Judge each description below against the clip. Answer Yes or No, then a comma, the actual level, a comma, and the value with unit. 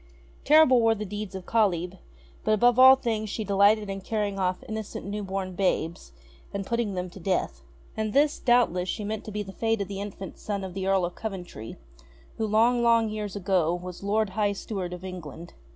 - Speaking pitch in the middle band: No, high, 200 Hz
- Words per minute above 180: Yes, average, 200 wpm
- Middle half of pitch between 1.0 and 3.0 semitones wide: Yes, average, 2.7 semitones